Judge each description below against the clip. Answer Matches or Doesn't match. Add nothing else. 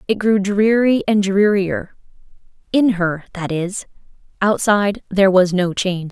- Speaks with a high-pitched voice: Matches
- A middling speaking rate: Doesn't match